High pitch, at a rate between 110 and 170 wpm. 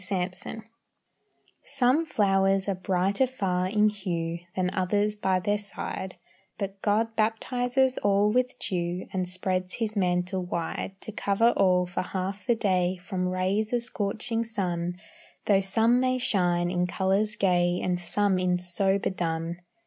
Yes: high, 195 Hz; average, 150 wpm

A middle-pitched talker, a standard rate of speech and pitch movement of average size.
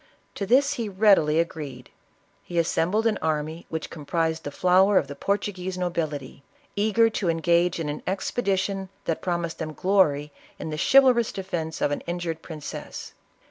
Yes: medium, 175 Hz; average, 160 wpm; average, 3.7 semitones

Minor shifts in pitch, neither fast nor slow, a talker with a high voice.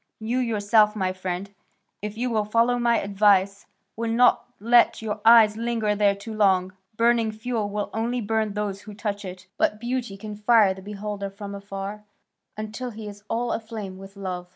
Yes: narrow, 2.3 semitones; average, 180 wpm; high, 210 Hz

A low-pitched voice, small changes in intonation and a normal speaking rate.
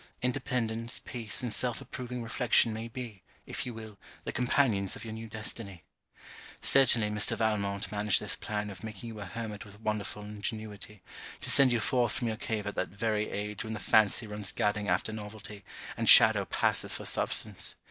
Yes: low, 110 Hz; narrow, 2.0 semitones; average, 180 wpm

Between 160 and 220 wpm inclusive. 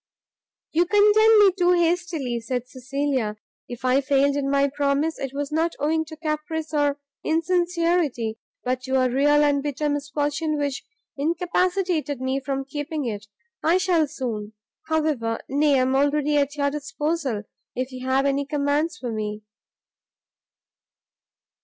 No: average, 145 wpm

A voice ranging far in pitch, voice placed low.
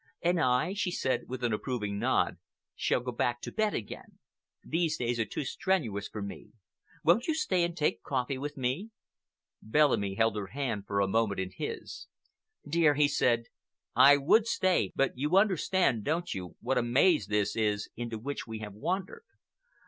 Yes: wide, 7.6 semitones; low, 130 Hz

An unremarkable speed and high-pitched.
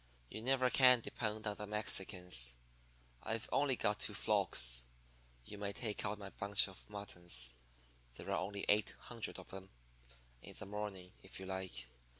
No: average, 160 wpm; low, 100 Hz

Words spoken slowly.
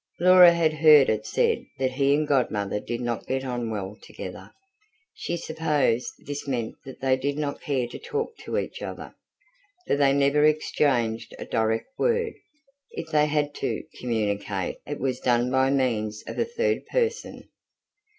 No: average, 165 wpm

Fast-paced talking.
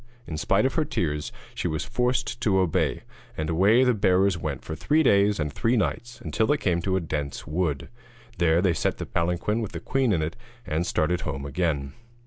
Yes: fast, 210 wpm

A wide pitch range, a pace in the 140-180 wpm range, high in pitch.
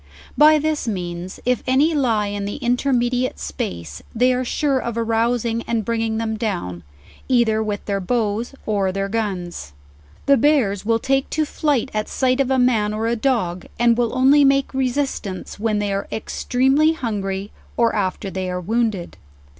No: average, 4.2 semitones; average, 170 wpm; high, 230 Hz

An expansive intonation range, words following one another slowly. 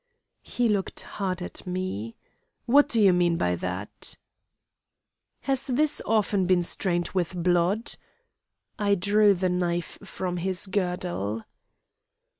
No: average, 2.9 semitones; slow, 120 wpm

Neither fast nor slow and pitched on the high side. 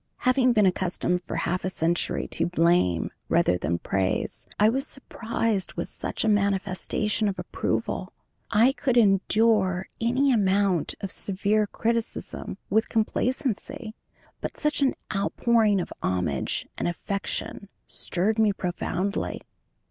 No: slow, 125 wpm; high, 200 Hz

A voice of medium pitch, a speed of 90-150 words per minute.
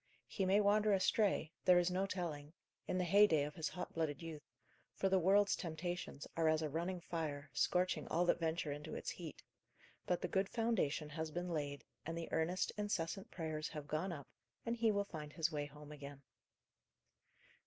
No: medium, 165 Hz; average, 185 wpm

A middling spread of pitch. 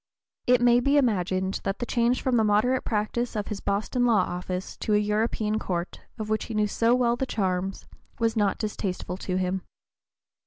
Yes: average, 3.6 semitones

